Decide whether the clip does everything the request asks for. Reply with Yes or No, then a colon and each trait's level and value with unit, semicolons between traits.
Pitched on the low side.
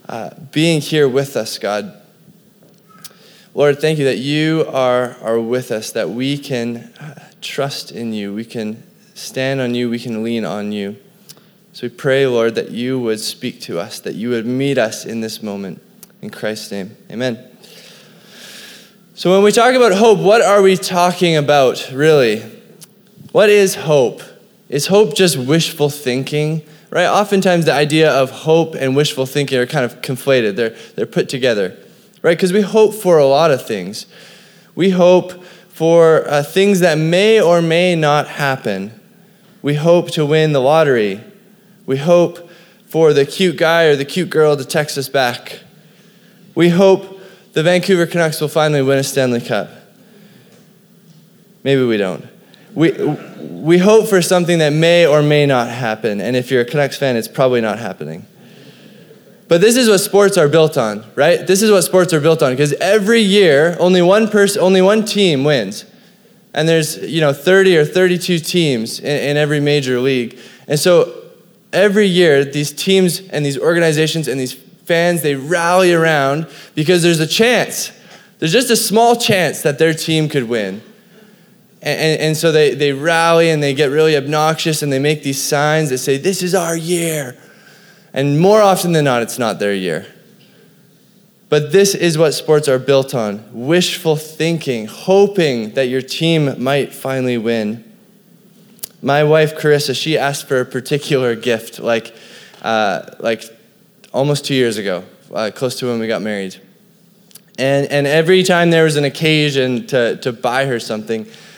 No: medium, 160 Hz